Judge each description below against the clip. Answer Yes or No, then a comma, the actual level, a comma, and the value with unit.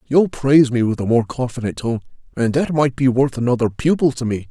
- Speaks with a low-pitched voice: Yes, low, 130 Hz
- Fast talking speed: Yes, fast, 225 wpm